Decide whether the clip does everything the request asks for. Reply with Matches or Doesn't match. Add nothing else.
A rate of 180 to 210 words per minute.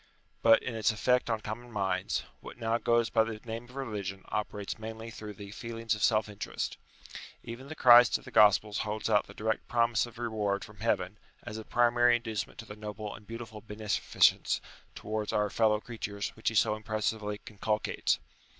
Matches